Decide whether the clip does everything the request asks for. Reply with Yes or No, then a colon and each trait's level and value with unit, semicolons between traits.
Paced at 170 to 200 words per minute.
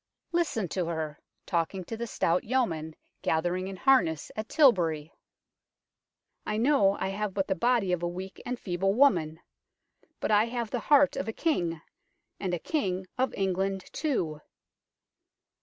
No: average, 155 wpm